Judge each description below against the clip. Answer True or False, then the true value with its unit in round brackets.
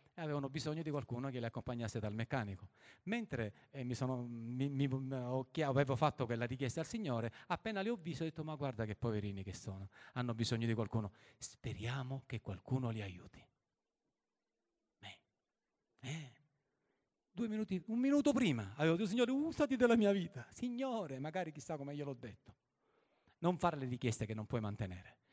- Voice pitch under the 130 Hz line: False (135 Hz)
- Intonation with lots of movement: True (5.9 semitones)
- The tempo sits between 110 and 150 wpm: False (170 wpm)